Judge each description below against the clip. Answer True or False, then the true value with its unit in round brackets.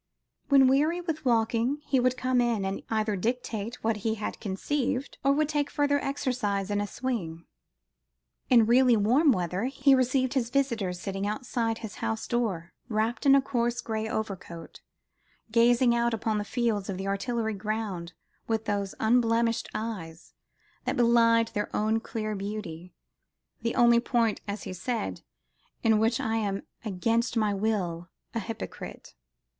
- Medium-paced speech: True (155 wpm)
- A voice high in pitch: True (225 Hz)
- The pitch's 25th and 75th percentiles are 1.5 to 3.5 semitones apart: True (3.2 semitones)